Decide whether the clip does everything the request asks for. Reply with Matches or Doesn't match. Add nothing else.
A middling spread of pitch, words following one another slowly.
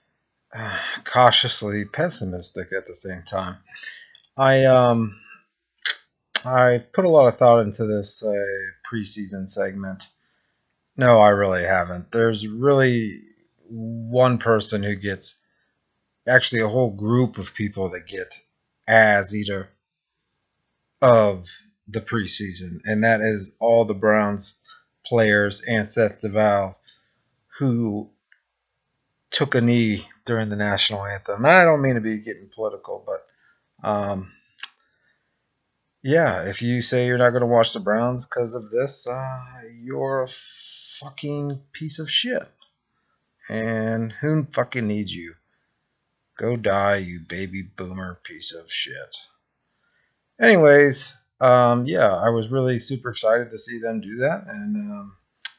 Matches